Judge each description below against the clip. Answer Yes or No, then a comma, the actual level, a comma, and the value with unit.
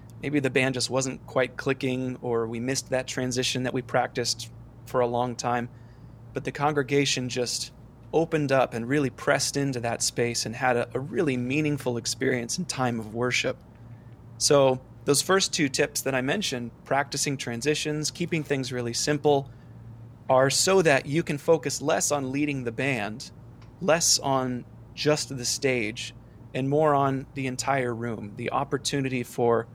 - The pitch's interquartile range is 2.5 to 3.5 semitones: Yes, average, 2.9 semitones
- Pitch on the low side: Yes, low, 130 Hz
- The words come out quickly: No, average, 165 wpm